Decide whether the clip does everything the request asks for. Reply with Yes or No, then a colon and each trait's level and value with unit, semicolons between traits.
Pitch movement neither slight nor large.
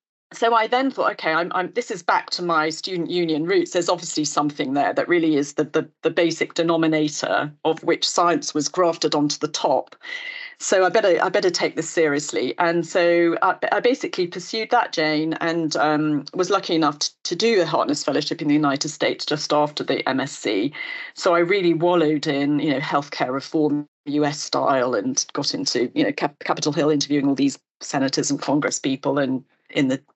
Yes: average, 3.5 semitones